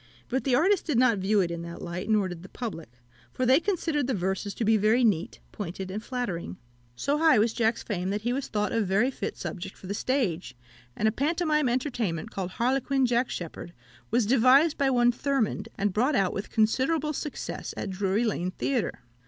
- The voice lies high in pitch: Yes, high, 225 Hz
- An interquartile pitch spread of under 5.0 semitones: No, wide, 5.4 semitones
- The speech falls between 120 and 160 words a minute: No, average, 200 wpm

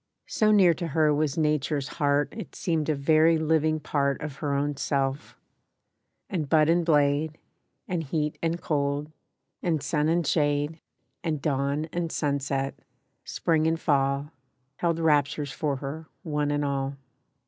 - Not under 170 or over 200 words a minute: No, average, 150 wpm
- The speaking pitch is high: No, medium, 150 Hz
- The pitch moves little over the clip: Yes, narrow, 2.2 semitones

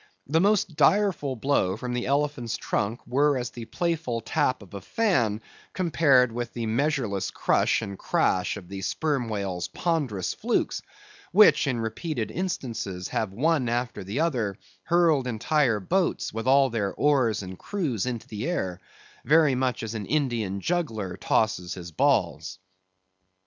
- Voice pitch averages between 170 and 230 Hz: No, low, 120 Hz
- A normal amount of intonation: No, wide, 6.0 semitones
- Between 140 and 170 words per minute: Yes, average, 150 wpm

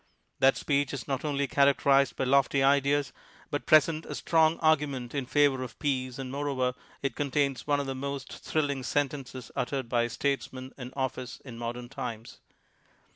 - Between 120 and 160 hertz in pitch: Yes, low, 135 Hz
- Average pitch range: No, narrow, 1.9 semitones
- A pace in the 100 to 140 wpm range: No, average, 175 wpm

